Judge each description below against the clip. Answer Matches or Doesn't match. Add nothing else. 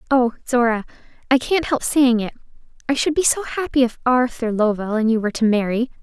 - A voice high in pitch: Matches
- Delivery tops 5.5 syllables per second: Matches